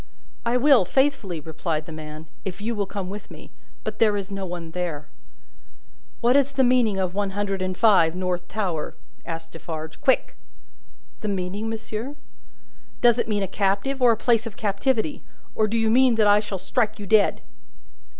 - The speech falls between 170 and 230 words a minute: Yes, average, 180 wpm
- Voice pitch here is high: Yes, high, 205 Hz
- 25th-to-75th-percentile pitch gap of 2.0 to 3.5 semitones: No, average, 4.1 semitones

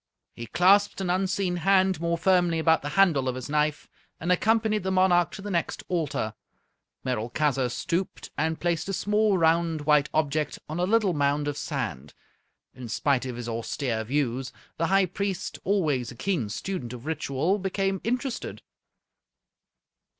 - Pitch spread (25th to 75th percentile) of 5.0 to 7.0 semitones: Yes, wide, 5.4 semitones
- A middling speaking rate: Yes, average, 155 wpm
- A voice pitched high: No, medium, 165 Hz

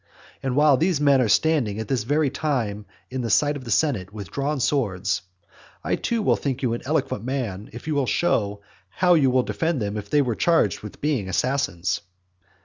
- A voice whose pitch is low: Yes, low, 130 Hz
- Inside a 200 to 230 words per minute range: Yes, fast, 205 wpm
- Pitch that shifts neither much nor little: No, wide, 5.8 semitones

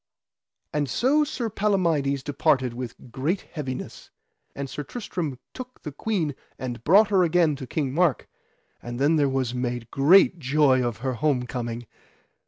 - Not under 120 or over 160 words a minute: Yes, average, 155 wpm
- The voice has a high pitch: No, medium, 140 Hz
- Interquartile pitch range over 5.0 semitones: Yes, wide, 5.5 semitones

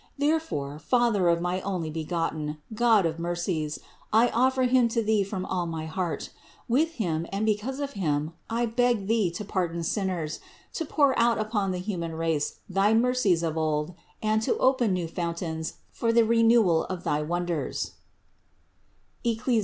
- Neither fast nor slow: Yes, average, 160 wpm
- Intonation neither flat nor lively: No, wide, 5.7 semitones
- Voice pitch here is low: No, high, 190 Hz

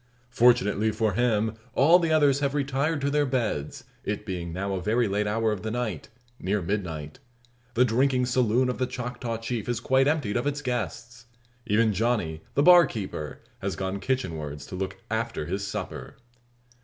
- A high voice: No, low, 115 Hz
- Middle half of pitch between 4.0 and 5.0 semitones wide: Yes, average, 4.5 semitones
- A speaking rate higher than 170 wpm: Yes, average, 180 wpm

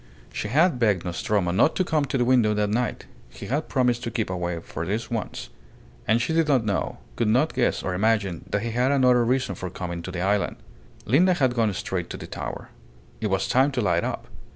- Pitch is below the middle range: Yes, low, 115 Hz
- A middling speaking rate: No, fast, 225 wpm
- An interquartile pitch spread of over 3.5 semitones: Yes, average, 5.0 semitones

